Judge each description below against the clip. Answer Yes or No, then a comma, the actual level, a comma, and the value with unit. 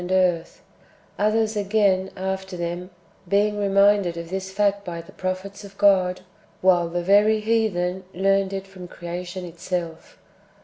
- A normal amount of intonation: No, narrow, 2.1 semitones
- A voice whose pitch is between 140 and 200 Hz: Yes, high, 190 Hz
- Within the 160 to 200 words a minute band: No, average, 140 wpm